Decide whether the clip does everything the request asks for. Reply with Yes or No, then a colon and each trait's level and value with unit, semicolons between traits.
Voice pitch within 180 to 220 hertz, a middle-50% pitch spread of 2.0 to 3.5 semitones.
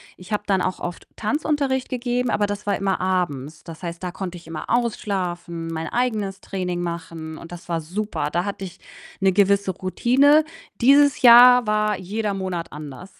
No: high, 190 Hz; average, 4.4 semitones